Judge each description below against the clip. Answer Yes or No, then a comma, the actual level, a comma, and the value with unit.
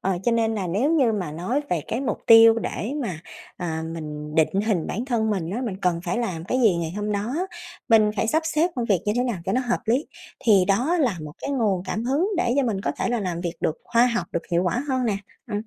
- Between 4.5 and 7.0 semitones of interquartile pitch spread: Yes, average, 5.2 semitones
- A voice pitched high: Yes, high, 215 Hz